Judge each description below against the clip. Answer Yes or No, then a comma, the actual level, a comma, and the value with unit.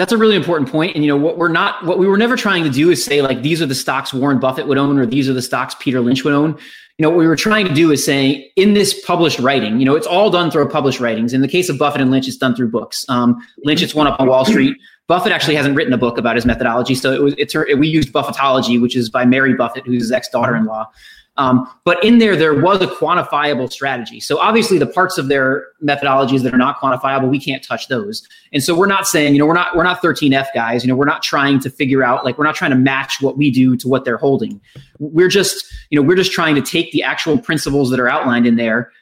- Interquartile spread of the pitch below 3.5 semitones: No, average, 4.2 semitones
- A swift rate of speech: Yes, fast, 280 wpm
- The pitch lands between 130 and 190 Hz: Yes, medium, 140 Hz